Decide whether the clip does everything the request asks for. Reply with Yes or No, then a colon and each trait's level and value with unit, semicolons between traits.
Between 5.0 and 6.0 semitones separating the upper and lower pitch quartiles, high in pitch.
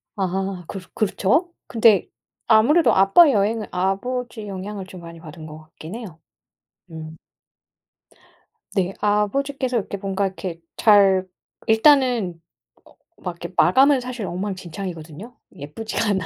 No: average, 4.1 semitones; high, 195 Hz